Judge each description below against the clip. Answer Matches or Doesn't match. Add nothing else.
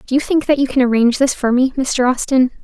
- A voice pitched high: Matches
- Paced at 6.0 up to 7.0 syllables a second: Matches